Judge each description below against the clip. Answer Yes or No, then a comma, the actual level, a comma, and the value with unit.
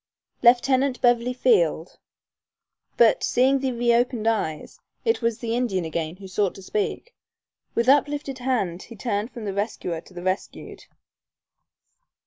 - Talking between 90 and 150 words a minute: Yes, slow, 135 wpm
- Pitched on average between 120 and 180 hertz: No, high, 235 Hz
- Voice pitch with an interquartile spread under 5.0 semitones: Yes, average, 4.6 semitones